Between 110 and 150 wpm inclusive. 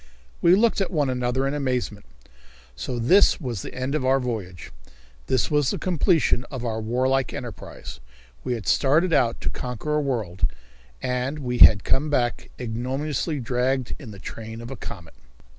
No: average, 170 wpm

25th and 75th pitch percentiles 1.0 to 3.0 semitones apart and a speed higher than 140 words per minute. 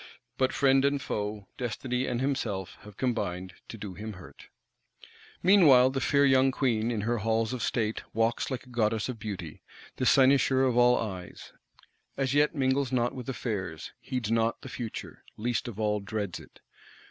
No: average, 3.6 semitones; average, 170 wpm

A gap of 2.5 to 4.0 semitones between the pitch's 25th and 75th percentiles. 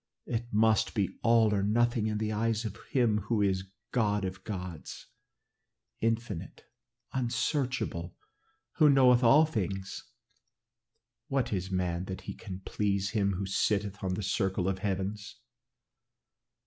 Yes: average, 3.3 semitones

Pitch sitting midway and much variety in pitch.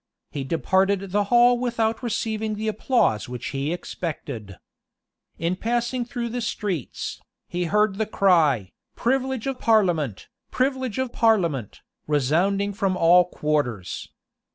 No: high, 200 Hz; wide, 6.8 semitones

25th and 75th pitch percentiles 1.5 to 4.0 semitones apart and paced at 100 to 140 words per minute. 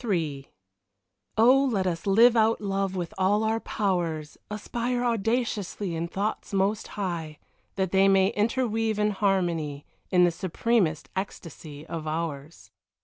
No: average, 4.5 semitones; slow, 135 wpm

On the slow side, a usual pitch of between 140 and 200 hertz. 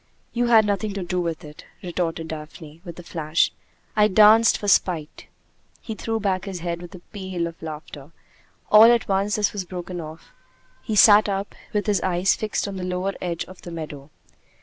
No: average, 195 wpm; medium, 185 Hz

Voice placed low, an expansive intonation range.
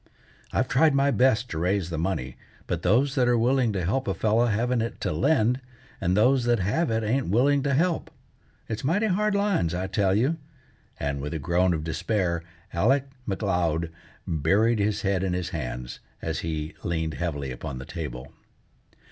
Yes: low, 105 Hz; wide, 7.3 semitones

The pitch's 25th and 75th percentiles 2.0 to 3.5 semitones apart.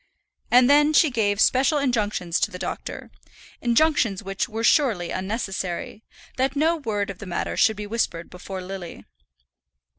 No: wide, 5.4 semitones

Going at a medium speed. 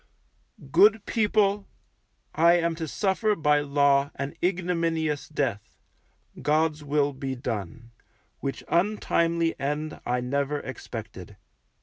No: slow, 105 wpm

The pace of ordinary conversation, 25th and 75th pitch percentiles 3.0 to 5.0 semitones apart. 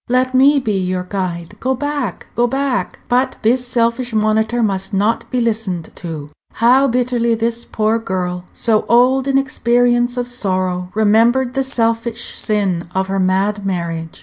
Yes: average, 155 wpm; average, 4.4 semitones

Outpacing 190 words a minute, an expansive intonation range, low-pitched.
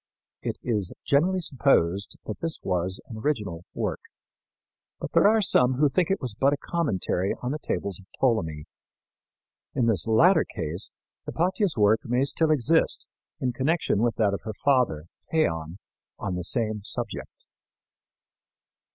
No: average, 150 wpm; wide, 7.4 semitones; low, 120 Hz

